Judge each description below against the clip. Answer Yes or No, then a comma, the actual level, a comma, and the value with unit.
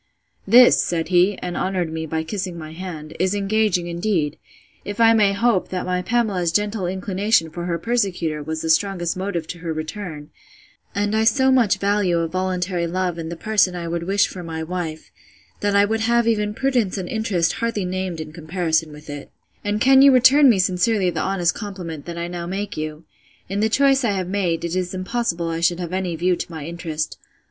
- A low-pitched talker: No, medium, 185 Hz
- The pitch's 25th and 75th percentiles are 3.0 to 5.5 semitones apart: Yes, average, 3.6 semitones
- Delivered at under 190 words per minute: No, average, 200 wpm